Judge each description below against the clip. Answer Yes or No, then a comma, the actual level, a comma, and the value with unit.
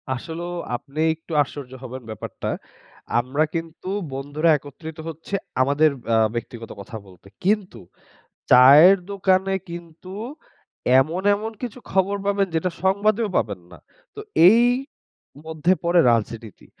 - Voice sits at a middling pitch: Yes, medium, 160 Hz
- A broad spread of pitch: Yes, wide, 6.3 semitones